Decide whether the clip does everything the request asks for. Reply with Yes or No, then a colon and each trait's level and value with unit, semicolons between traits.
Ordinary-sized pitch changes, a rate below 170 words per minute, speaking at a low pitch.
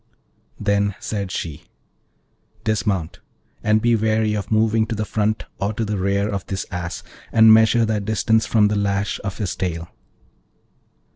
No: narrow, 1.8 semitones; average, 155 wpm; low, 105 Hz